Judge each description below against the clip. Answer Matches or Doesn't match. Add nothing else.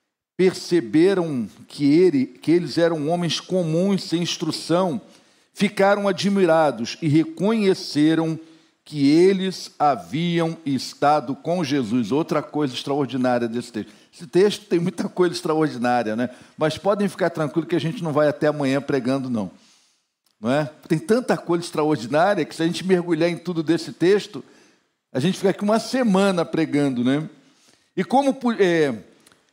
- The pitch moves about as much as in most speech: Matches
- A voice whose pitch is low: Doesn't match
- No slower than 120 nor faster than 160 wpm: Matches